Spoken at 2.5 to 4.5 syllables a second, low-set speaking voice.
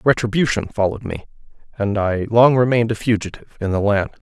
No: 6.3 syllables/s; low, 110 Hz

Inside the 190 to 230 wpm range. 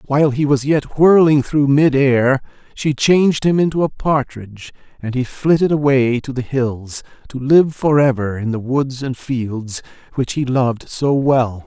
No: average, 170 wpm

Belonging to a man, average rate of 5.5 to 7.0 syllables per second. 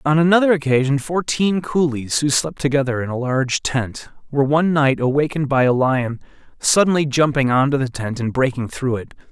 Yes: male; 5.6 syllables/s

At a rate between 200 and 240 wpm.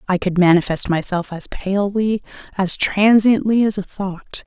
No: average, 150 wpm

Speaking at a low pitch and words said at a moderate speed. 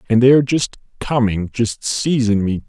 Yes: low, 115 Hz; average, 180 wpm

